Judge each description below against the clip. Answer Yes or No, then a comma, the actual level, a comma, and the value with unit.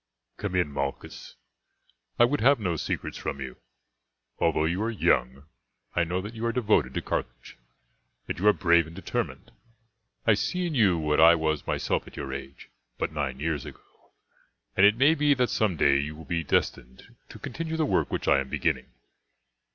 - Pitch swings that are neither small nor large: No, wide, 7.4 semitones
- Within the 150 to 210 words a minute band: Yes, average, 190 wpm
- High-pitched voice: No, very low, 85 Hz